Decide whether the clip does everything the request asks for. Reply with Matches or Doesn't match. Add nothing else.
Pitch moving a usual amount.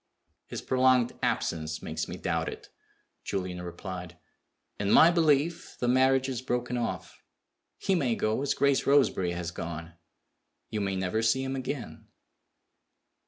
Doesn't match